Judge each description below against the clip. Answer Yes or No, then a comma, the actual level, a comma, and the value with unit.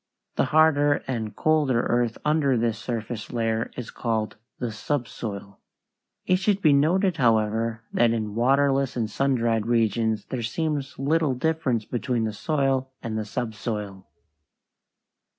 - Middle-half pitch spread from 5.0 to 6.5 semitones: No, average, 4.1 semitones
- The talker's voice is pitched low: Yes, low, 120 Hz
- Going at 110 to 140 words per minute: Yes, slow, 135 wpm